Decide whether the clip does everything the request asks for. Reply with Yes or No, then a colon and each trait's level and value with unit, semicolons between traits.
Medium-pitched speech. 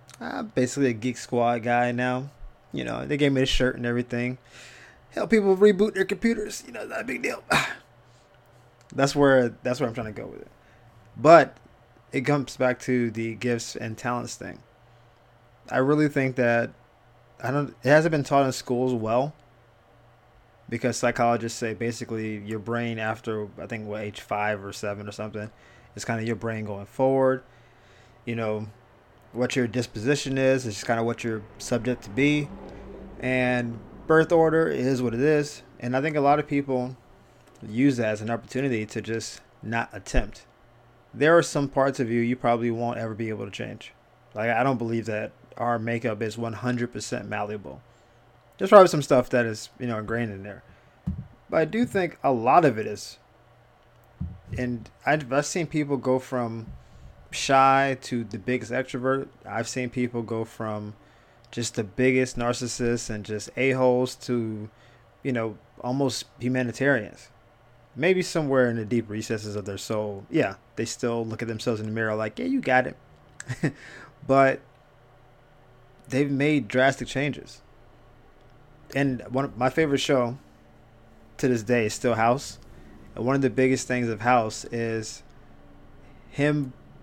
No: low, 120 Hz